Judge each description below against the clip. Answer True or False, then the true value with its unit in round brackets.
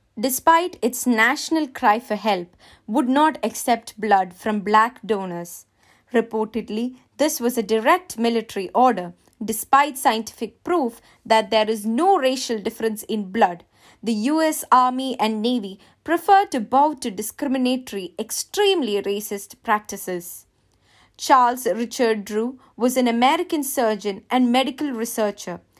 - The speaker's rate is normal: False (130 wpm)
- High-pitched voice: True (230 Hz)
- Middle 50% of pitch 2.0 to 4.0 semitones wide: True (3.7 semitones)